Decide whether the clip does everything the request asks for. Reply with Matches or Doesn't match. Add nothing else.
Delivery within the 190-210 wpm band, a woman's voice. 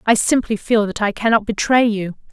Matches